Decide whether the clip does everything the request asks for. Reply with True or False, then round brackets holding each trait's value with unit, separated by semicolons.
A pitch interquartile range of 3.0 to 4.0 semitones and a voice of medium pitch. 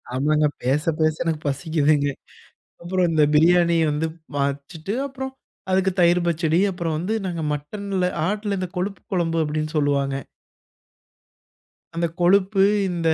True (3.5 semitones; 165 Hz)